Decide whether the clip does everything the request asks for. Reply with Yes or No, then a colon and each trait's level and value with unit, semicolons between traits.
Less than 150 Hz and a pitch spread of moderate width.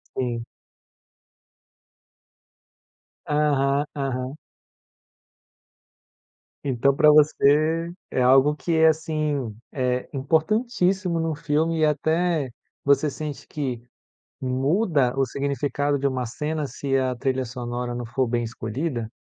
Yes: medium, 140 Hz; average, 3.3 semitones